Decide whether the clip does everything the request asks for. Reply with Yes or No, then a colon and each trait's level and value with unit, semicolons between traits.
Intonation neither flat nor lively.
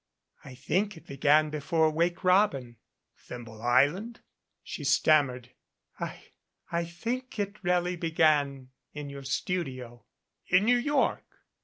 Yes: average, 4.9 semitones